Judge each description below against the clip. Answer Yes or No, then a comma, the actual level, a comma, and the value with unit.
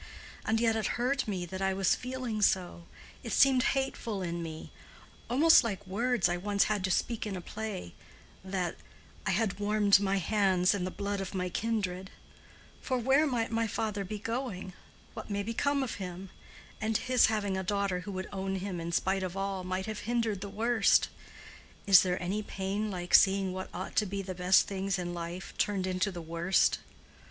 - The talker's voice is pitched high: Yes, high, 195 Hz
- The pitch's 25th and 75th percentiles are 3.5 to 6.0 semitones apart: No, average, 3.0 semitones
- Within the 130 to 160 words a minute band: No, average, 185 wpm